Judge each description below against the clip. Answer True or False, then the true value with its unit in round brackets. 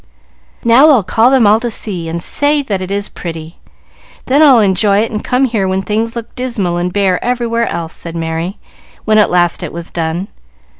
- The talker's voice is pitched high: True (205 Hz)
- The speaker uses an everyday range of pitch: True (5.0 semitones)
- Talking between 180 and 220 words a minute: True (200 wpm)